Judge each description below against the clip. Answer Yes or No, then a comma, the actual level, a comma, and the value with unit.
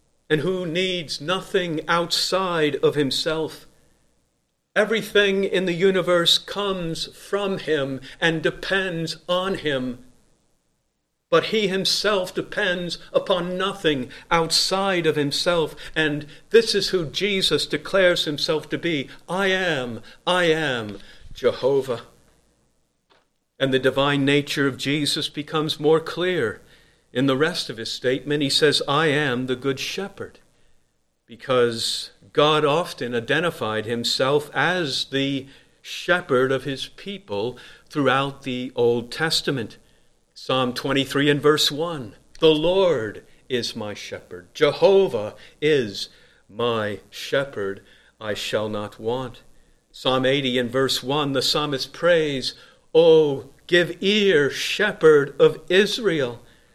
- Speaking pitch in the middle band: Yes, medium, 155 Hz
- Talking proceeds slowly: Yes, slow, 115 wpm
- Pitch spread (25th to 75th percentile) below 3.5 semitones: No, average, 5.2 semitones